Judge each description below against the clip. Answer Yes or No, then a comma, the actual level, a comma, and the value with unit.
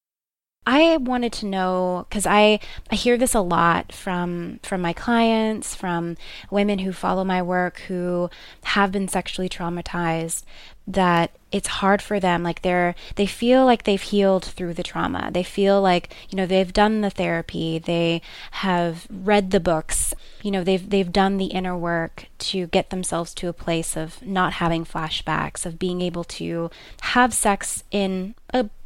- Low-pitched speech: No, medium, 185 Hz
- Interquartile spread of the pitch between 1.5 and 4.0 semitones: Yes, average, 2.8 semitones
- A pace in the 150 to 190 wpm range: Yes, average, 170 wpm